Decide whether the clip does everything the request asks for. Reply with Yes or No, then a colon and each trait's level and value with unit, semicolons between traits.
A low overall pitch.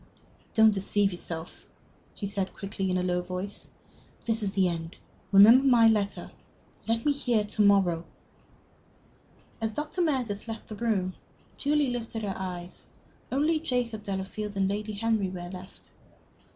No: high, 205 Hz